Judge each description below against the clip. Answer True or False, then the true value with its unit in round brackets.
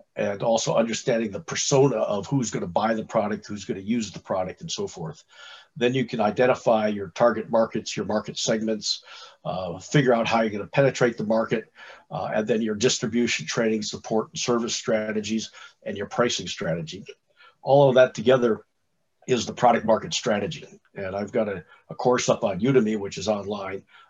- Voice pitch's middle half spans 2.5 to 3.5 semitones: True (3.1 semitones)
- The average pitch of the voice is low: True (115 Hz)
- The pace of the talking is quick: False (180 wpm)